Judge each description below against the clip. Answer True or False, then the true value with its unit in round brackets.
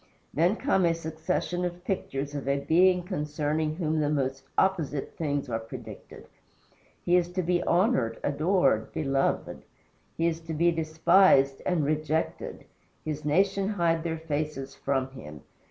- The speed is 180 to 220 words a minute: False (145 wpm)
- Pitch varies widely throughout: False (3.8 semitones)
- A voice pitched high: False (155 Hz)